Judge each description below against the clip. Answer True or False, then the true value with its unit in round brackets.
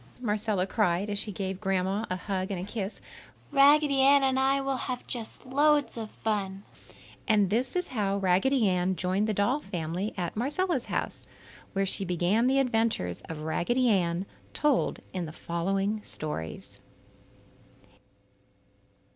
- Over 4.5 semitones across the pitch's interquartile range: True (5.6 semitones)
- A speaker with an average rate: True (145 wpm)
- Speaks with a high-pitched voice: True (205 Hz)